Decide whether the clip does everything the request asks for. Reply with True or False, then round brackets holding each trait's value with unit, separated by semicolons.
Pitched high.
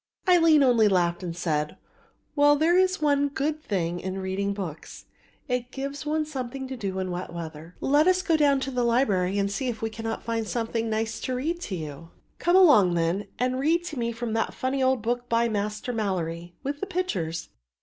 True (235 Hz)